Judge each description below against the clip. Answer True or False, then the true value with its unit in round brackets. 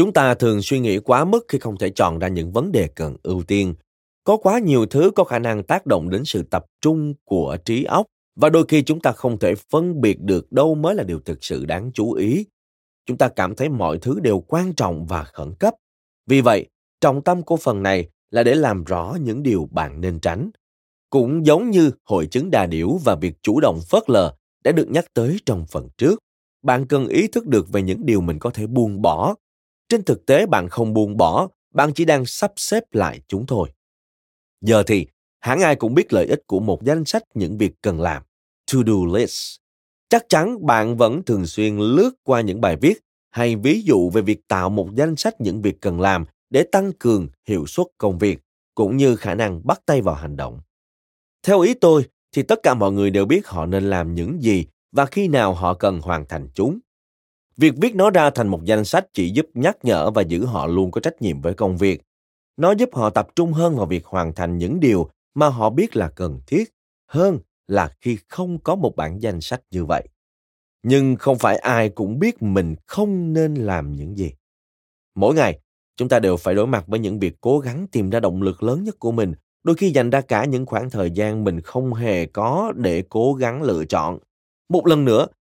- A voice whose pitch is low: True (105 Hz)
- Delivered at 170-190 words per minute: False (220 wpm)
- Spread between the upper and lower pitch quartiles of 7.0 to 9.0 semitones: True (8.2 semitones)